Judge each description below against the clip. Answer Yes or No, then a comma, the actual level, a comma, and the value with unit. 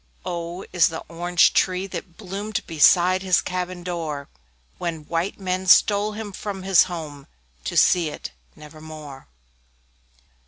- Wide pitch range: No, narrow, 2.5 semitones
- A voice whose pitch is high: No, medium, 175 Hz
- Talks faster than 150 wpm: No, average, 145 wpm